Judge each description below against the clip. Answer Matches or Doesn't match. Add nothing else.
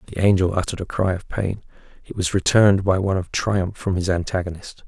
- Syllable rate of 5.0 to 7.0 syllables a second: Matches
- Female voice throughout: Doesn't match